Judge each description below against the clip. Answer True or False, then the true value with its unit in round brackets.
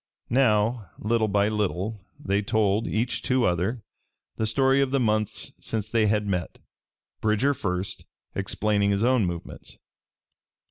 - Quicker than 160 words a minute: False (135 wpm)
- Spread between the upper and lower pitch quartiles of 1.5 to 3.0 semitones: True (2.7 semitones)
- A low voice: True (110 Hz)